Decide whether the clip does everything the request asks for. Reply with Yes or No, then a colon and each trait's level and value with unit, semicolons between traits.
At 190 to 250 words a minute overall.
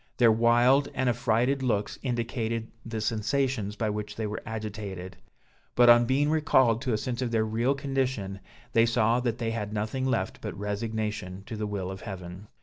No: average, 180 wpm